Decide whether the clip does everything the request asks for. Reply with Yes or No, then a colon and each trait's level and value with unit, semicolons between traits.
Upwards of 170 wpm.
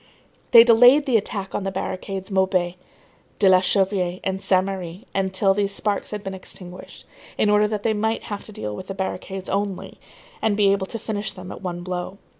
Yes: average, 200 wpm